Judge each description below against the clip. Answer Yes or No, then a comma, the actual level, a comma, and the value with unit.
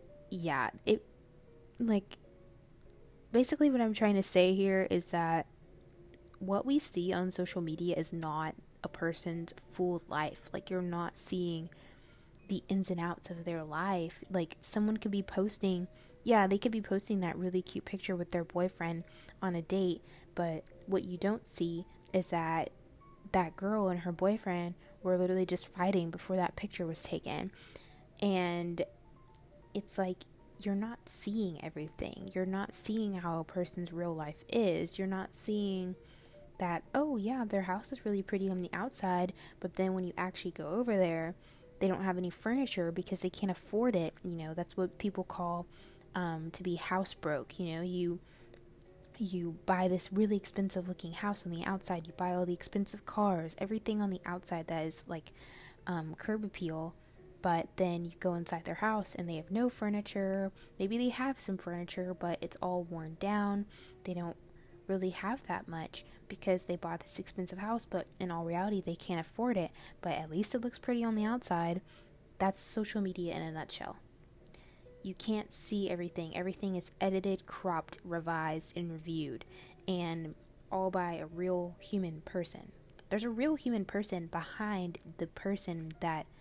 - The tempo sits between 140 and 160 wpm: No, average, 170 wpm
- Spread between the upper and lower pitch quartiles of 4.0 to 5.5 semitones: No, average, 2.7 semitones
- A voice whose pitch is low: No, medium, 180 Hz